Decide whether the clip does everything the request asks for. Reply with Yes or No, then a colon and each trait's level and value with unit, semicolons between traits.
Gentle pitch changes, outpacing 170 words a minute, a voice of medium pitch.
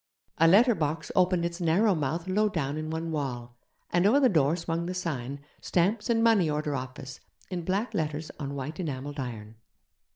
No: average, 4.6 semitones; average, 185 wpm; medium, 165 Hz